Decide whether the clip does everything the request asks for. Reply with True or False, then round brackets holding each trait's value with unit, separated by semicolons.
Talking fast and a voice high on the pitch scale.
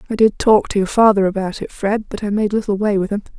True (285 wpm; 210 Hz)